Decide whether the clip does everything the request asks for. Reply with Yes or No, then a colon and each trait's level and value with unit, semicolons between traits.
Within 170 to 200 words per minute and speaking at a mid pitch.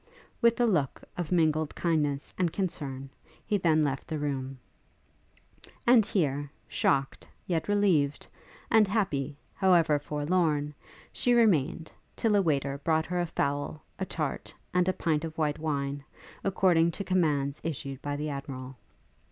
No: average, 145 wpm; medium, 155 Hz